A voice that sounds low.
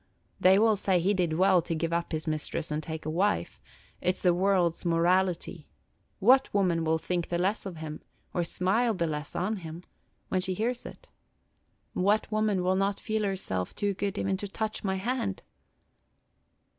No: medium, 185 Hz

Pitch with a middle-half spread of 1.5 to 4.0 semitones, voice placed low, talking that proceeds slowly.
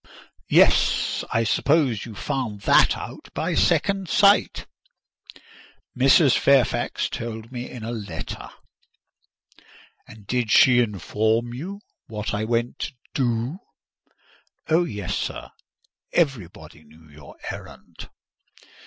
No: average, 4.4 semitones; low, 120 Hz; slow, 110 wpm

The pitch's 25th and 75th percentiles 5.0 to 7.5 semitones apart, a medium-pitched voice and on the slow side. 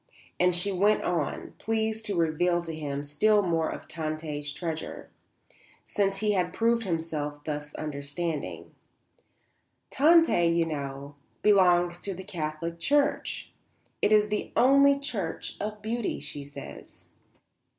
Yes: wide, 5.5 semitones; medium, 175 Hz; slow, 130 wpm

